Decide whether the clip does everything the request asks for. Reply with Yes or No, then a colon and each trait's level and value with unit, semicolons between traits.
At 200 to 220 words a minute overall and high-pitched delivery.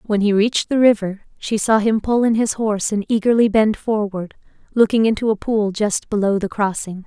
Yes: fast, 205 wpm; high, 215 Hz